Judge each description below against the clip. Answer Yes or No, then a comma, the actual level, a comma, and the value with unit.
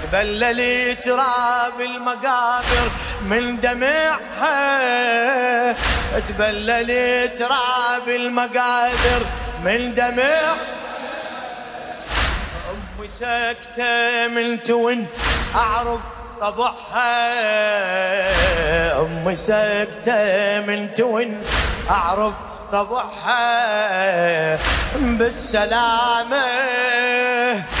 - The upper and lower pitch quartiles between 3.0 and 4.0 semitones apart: No, narrow, 2.5 semitones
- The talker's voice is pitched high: Yes, high, 240 Hz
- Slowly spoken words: Yes, slow, 50 wpm